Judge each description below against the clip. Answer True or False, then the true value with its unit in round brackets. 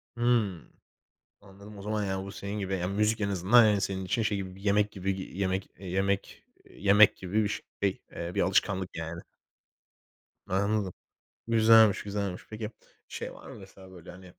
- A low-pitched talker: True (100 Hz)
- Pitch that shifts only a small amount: True (1.9 semitones)